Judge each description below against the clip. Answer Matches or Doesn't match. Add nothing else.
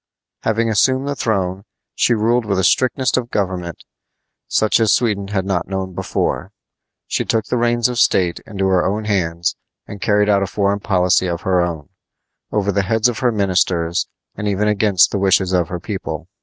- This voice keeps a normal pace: Matches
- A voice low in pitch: Matches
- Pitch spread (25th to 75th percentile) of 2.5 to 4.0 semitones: Matches